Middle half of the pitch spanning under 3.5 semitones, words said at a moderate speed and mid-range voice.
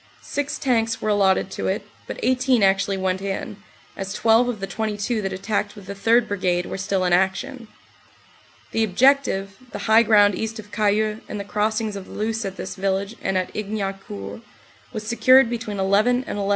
No: narrow, 2.6 semitones; average, 190 wpm; high, 205 Hz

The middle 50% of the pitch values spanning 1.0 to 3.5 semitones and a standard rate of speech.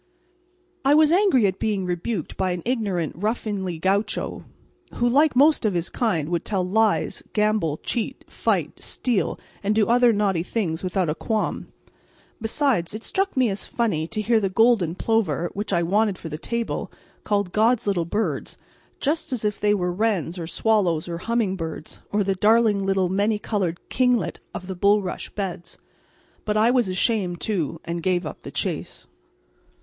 No: average, 4.0 semitones; average, 170 wpm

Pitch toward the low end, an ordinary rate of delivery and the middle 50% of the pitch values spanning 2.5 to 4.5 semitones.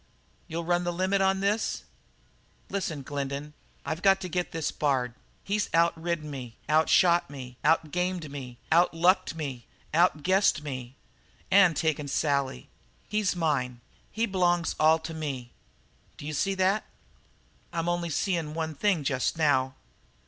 No: medium, 160 Hz; average, 150 wpm; average, 4.0 semitones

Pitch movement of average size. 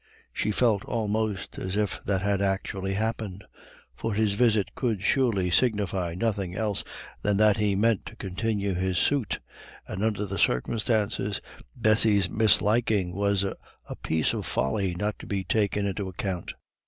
No: narrow, 2.3 semitones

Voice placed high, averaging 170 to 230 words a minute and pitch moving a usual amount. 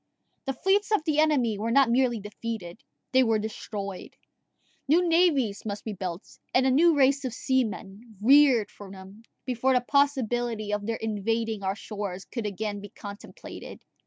No: high, 230 Hz; average, 160 wpm; average, 4.4 semitones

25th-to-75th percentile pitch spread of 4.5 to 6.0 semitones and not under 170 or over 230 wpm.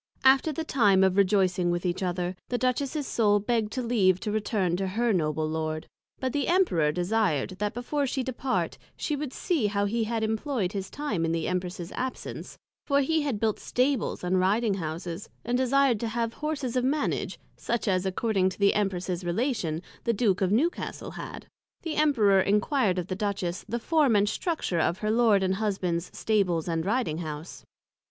Yes: wide, 5.4 semitones; average, 180 wpm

